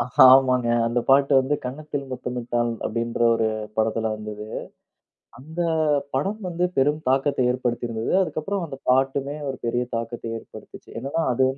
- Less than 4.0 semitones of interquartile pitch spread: Yes, average, 3.3 semitones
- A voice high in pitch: No, low, 130 Hz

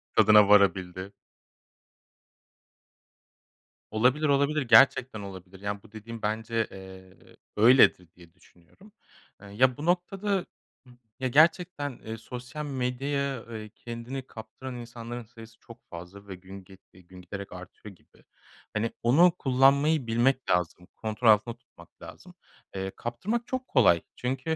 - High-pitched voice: No, low, 115 Hz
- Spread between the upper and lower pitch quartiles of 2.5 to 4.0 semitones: No, average, 5.1 semitones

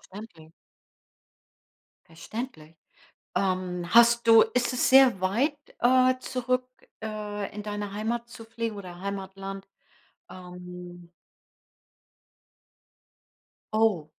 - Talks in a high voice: Yes, high, 210 Hz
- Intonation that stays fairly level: No, average, 4.3 semitones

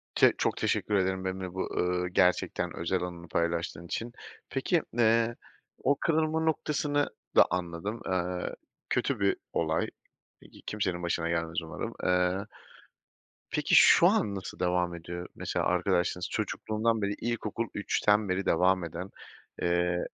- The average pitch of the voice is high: No, very low, 90 Hz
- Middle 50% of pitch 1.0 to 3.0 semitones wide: No, average, 3.7 semitones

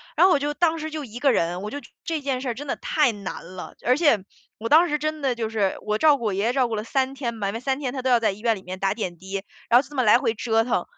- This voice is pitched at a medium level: No, high, 240 Hz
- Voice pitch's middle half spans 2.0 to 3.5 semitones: No, average, 5.0 semitones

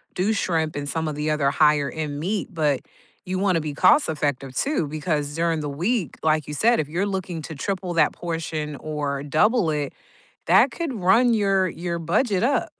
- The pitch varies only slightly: No, average, 4.3 semitones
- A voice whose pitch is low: No, medium, 165 Hz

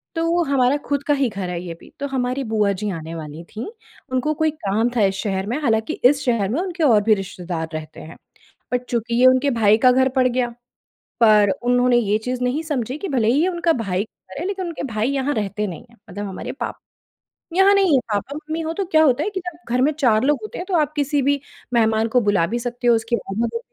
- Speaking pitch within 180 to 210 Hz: No, high, 245 Hz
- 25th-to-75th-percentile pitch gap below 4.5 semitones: No, average, 5.3 semitones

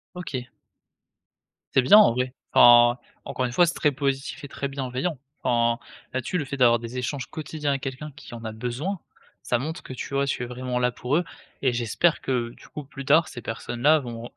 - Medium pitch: No, low, 130 Hz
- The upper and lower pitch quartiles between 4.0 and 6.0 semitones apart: No, average, 3.1 semitones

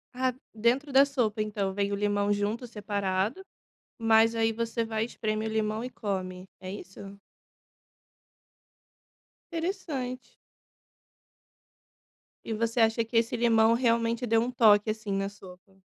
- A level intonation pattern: Yes, narrow, 2.3 semitones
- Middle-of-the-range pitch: No, high, 220 Hz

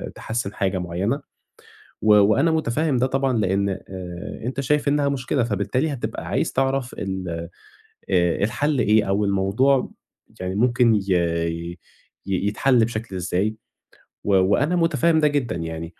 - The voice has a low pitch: Yes, low, 110 Hz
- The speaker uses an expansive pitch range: Yes, wide, 5.9 semitones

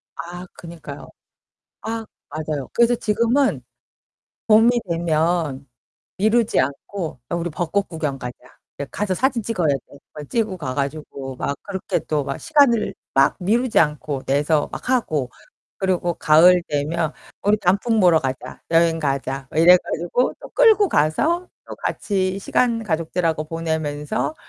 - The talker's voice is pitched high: No, medium, 170 Hz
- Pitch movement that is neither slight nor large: No, wide, 6.0 semitones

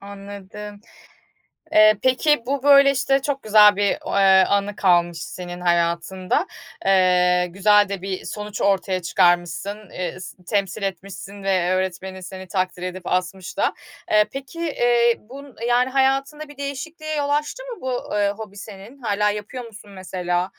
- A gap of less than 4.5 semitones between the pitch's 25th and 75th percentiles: No, average, 5.1 semitones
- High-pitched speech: Yes, high, 200 Hz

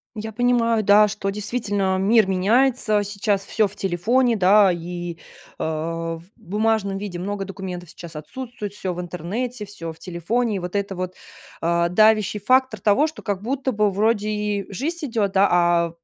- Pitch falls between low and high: No, high, 200 Hz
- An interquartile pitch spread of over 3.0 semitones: Yes, average, 3.7 semitones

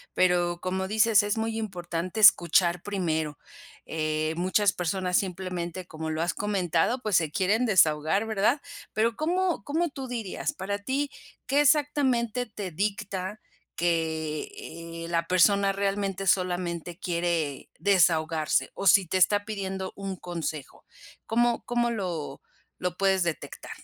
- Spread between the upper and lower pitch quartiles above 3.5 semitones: Yes, average, 3.9 semitones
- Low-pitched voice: No, high, 190 Hz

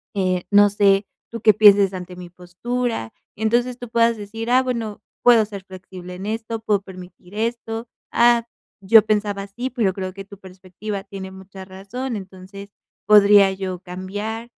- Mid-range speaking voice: No, high, 200 Hz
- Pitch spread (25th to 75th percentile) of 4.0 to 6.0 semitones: No, average, 3.0 semitones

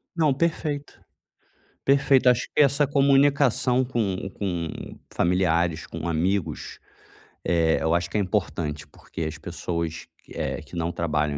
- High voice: No, very low, 90 Hz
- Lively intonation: Yes, wide, 8.6 semitones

